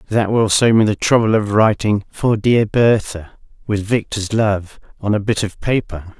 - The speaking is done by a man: Yes, male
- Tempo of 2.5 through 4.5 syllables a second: Yes, 4.4 syllables/s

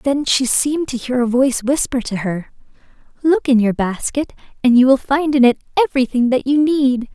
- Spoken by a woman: Yes, female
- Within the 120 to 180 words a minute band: No, average, 200 wpm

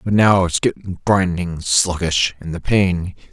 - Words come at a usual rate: Yes, average, 165 wpm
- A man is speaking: Yes, male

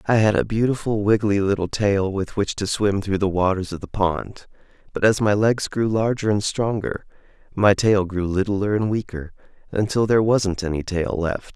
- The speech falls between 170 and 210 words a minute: Yes, average, 190 wpm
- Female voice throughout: No, male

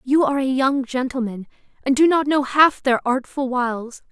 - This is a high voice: Yes, very high, 265 Hz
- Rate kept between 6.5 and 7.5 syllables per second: No, 5.1 syllables/s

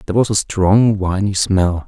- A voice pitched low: Yes, low, 100 Hz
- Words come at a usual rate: Yes, average, 190 wpm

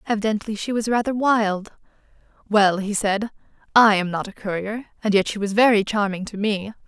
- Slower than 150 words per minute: No, average, 185 wpm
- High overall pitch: Yes, high, 210 Hz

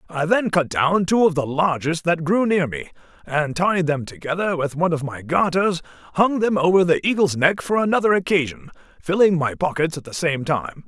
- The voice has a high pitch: No, medium, 165 Hz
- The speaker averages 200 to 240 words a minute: Yes, fast, 205 wpm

